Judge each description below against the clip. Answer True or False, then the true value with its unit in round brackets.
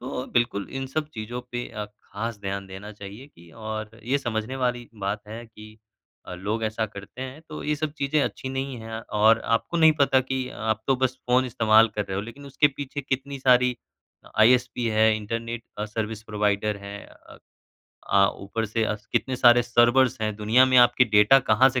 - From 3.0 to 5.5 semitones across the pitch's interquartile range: True (3.4 semitones)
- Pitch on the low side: True (115 Hz)